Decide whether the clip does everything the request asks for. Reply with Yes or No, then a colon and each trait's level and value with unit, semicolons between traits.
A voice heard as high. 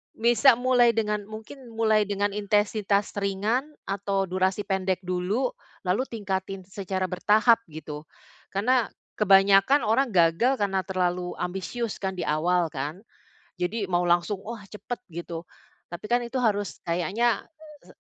Yes: high, 200 Hz